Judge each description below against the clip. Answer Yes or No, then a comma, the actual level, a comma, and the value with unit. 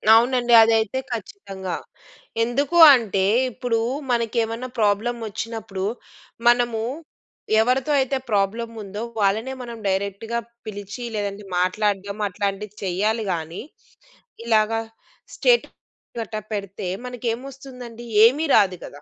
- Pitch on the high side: Yes, high, 225 Hz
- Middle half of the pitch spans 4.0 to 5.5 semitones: No, average, 3.3 semitones